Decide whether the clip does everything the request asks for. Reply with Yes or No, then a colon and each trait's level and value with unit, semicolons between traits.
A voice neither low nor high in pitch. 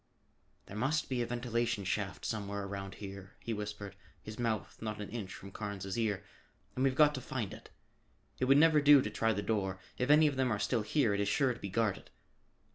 No: low, 110 Hz